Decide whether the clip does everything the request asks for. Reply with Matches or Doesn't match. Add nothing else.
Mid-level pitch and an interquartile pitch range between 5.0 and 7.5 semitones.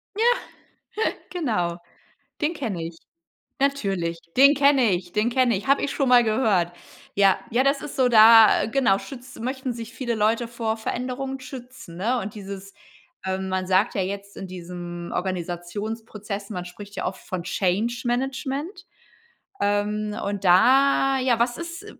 Doesn't match